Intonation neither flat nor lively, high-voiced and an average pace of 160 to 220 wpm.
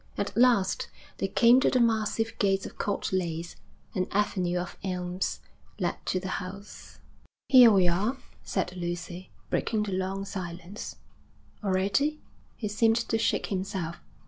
No: average, 3.2 semitones; high, 195 Hz; average, 145 wpm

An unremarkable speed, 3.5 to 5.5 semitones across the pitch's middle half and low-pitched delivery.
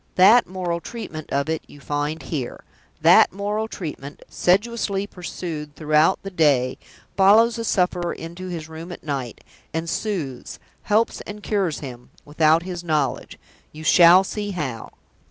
No: average, 150 wpm; average, 4.5 semitones; medium, 170 Hz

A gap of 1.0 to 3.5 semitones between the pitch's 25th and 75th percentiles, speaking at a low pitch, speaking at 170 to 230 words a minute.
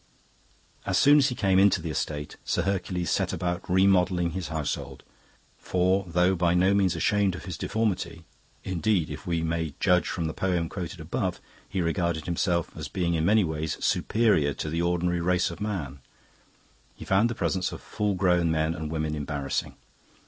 Yes: average, 2.7 semitones; very low, 90 Hz; average, 180 wpm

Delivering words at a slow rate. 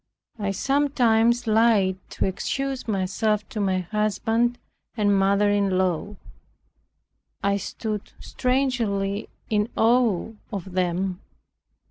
Yes: slow, 100 wpm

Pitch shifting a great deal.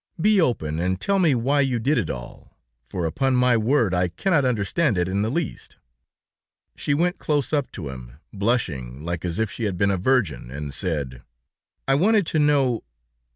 Yes: wide, 8.7 semitones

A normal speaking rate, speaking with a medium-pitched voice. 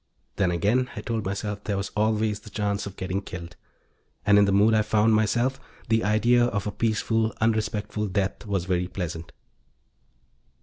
No: average, 170 wpm; low, 105 Hz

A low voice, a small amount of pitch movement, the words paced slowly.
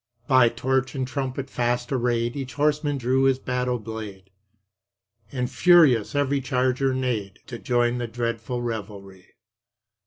Yes: low, 125 Hz; narrow, 2.2 semitones; slow, 130 wpm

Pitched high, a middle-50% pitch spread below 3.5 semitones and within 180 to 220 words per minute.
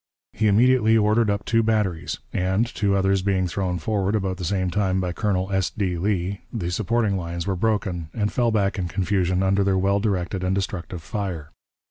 No: very low, 95 Hz; narrow, 2.4 semitones; average, 190 wpm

